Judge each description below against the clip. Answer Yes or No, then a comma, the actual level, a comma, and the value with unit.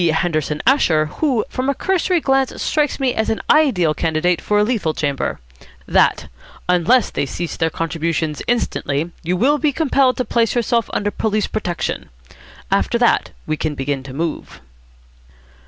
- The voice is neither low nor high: No, high, 200 Hz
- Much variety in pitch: Yes, wide, 8.2 semitones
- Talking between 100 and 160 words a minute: Yes, average, 155 wpm